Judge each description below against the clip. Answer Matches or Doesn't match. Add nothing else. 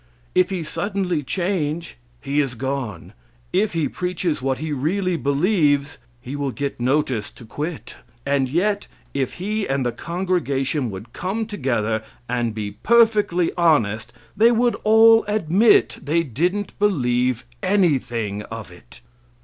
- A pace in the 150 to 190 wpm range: Doesn't match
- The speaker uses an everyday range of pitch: Doesn't match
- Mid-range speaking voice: Matches